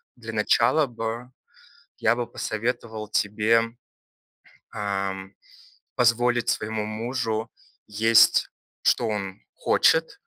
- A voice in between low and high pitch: No, low, 110 Hz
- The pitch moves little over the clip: Yes, narrow, 2.1 semitones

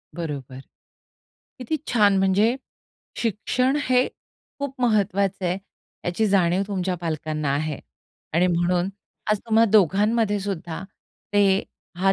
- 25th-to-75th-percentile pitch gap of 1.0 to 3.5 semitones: No, average, 4.0 semitones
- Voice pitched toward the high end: Yes, high, 195 Hz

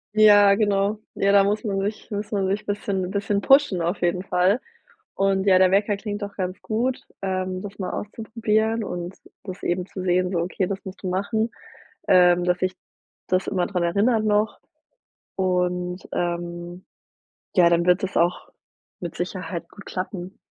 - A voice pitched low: No, high, 190 Hz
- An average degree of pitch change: No, narrow, 2.3 semitones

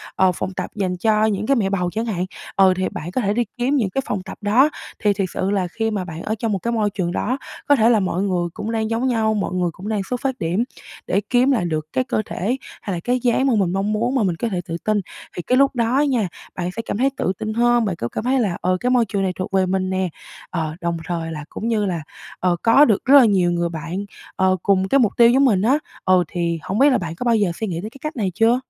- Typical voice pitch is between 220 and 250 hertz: No, high, 205 Hz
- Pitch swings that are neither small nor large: Yes, average, 4.4 semitones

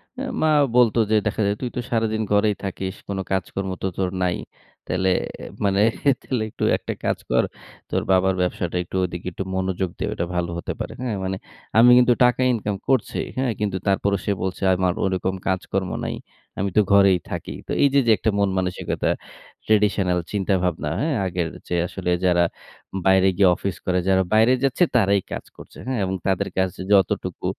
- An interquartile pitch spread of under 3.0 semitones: Yes, narrow, 2.6 semitones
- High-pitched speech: No, very low, 95 Hz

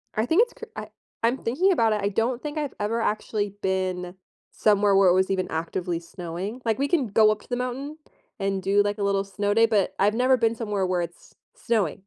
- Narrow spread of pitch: No, average, 3.7 semitones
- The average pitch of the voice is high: Yes, high, 210 Hz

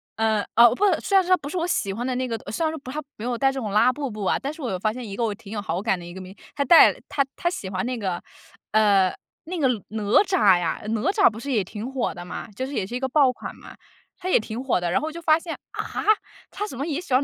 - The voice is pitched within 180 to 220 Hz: No, high, 245 Hz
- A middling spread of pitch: No, wide, 5.7 semitones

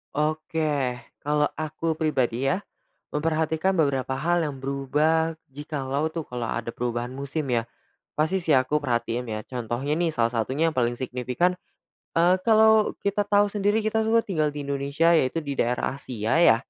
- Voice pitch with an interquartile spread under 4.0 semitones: No, average, 4.3 semitones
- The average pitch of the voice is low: No, medium, 150 Hz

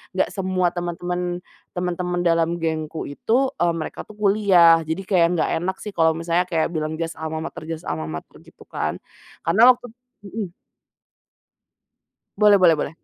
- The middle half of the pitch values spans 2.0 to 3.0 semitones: Yes, narrow, 2.6 semitones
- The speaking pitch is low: No, medium, 175 Hz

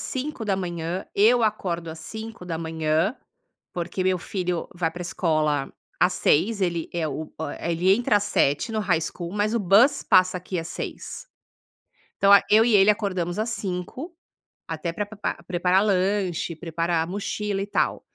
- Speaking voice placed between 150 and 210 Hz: Yes, medium, 185 Hz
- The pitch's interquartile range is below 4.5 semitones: Yes, average, 3.5 semitones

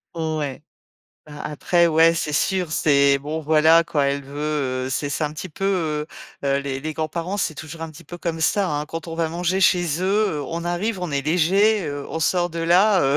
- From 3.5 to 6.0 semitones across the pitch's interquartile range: No, average, 2.9 semitones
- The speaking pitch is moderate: Yes, medium, 160 Hz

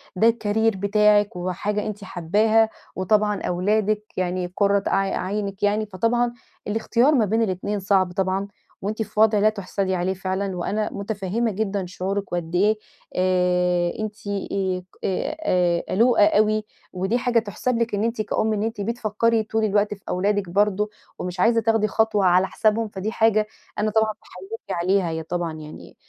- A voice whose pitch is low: No, high, 205 Hz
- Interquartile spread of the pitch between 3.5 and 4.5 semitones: No, average, 2.7 semitones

